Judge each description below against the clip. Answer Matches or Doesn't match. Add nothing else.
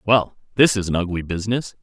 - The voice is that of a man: Matches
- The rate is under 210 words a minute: Matches